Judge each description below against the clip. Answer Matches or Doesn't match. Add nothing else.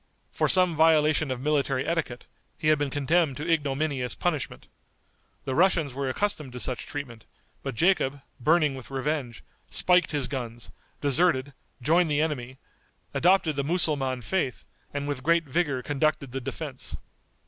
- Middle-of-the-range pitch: Matches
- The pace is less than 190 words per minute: Matches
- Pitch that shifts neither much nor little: Matches